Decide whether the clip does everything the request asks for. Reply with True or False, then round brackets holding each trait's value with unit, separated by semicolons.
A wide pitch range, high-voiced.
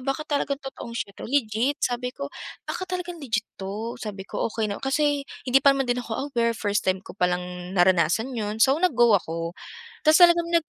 True (5.7 semitones; 240 Hz)